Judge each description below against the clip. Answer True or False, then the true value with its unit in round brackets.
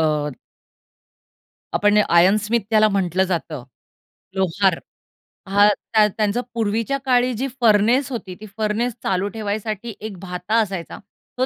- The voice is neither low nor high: False (210 Hz)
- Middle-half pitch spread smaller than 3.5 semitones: True (2.9 semitones)